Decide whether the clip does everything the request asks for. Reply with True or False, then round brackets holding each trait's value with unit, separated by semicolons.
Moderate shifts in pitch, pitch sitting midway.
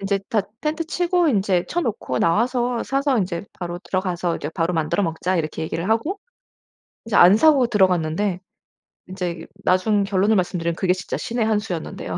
False (4.7 semitones; 195 Hz)